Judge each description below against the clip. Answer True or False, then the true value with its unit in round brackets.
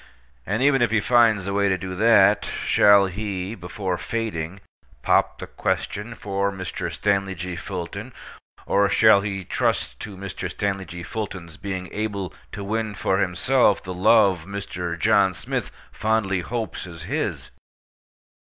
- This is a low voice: True (100 Hz)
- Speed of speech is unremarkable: True (150 wpm)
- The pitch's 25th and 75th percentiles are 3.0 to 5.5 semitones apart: False (2.4 semitones)